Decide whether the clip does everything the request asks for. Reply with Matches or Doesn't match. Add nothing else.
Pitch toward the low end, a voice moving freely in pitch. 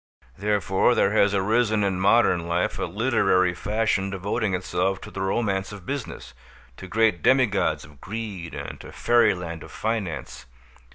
Doesn't match